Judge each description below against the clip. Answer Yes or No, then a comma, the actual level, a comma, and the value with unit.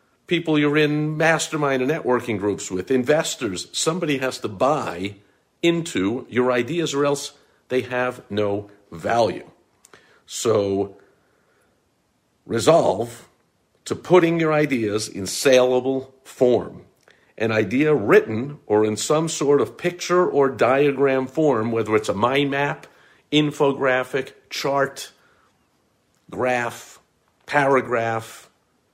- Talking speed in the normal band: No, slow, 110 wpm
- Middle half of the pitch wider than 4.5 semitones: Yes, average, 5.0 semitones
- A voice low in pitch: Yes, low, 130 Hz